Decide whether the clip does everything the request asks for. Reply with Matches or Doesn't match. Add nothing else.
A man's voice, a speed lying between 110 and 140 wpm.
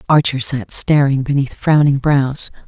Doesn't match